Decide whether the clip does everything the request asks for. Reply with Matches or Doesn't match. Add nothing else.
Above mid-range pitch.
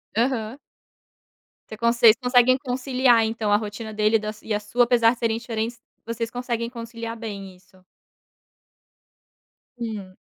Matches